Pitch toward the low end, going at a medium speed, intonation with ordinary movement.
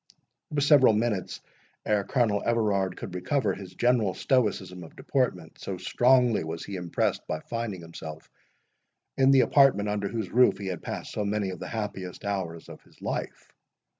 Yes: low, 100 Hz; average, 170 wpm; average, 4.5 semitones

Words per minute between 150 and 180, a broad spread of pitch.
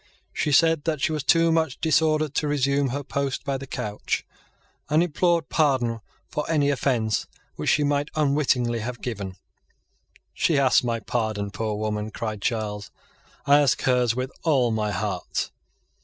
No: average, 155 wpm; average, 5.0 semitones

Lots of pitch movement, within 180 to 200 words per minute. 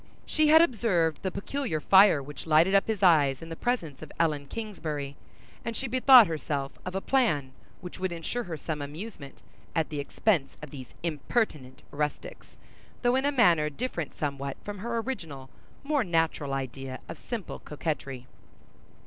No: wide, 7.6 semitones; average, 165 wpm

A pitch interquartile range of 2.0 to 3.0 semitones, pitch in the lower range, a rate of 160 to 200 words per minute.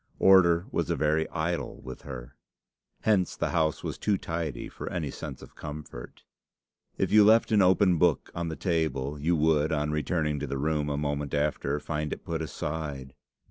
Yes: average, 2.7 semitones; very low, 75 Hz; average, 180 wpm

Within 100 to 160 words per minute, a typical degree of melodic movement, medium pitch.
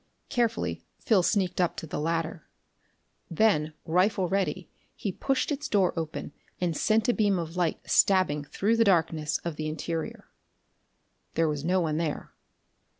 Yes: average, 150 wpm; average, 4.0 semitones; medium, 175 Hz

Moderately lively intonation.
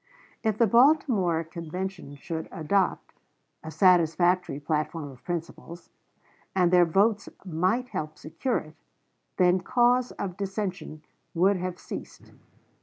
Yes: average, 3.7 semitones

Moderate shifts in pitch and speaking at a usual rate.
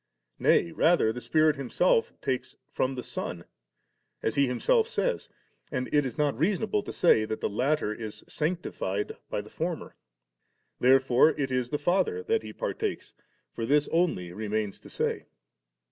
No: wide, 7.0 semitones; average, 160 wpm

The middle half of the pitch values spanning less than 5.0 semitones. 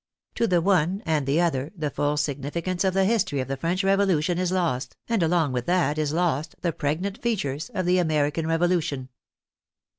Yes: average, 3.9 semitones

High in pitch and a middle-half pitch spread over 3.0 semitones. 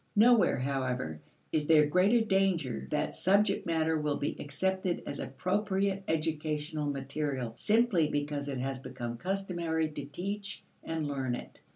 No: medium, 155 Hz; average, 5.1 semitones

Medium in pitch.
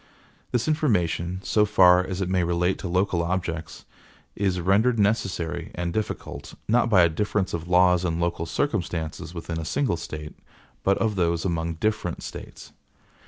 No: very low, 90 Hz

